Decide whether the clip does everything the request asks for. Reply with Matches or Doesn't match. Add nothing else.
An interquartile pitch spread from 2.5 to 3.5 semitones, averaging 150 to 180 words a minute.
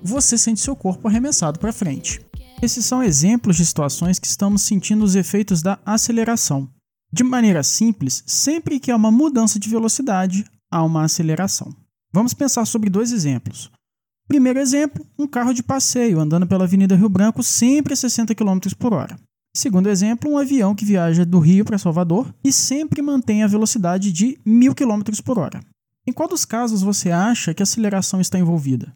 Doesn't match